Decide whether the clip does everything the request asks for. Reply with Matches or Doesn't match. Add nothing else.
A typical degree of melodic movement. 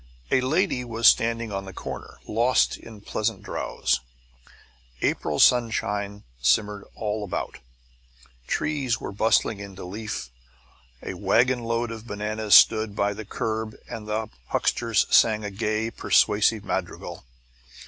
Doesn't match